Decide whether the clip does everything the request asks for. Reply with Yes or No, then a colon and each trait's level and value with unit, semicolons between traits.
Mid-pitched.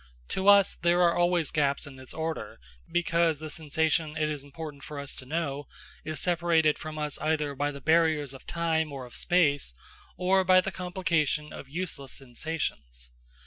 Yes: medium, 155 Hz